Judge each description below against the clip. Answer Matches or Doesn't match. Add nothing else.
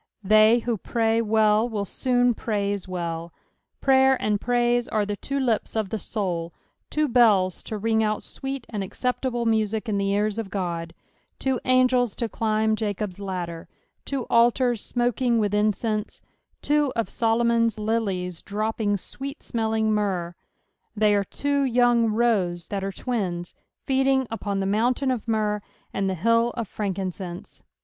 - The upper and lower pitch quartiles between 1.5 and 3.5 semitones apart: Matches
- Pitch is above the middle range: Matches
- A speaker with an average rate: Matches